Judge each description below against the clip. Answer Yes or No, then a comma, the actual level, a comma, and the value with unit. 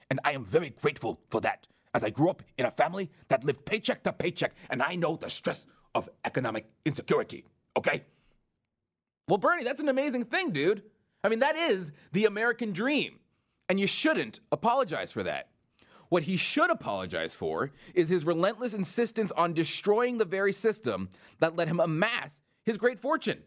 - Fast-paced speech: No, average, 175 wpm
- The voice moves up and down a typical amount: No, wide, 6.3 semitones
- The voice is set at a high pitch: Yes, high, 195 Hz